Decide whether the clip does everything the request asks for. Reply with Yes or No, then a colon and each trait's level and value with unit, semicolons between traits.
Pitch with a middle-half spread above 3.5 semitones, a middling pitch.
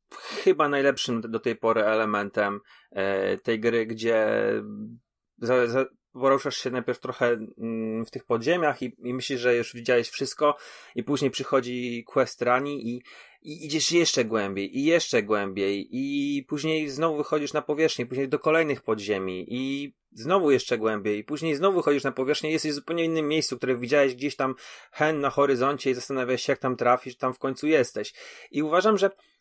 No: average, 4.3 semitones; low, 130 Hz